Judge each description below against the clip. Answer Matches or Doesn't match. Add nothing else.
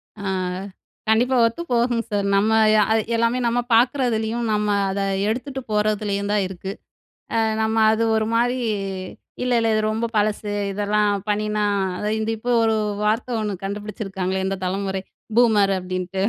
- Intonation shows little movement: Matches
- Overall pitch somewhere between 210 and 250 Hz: Matches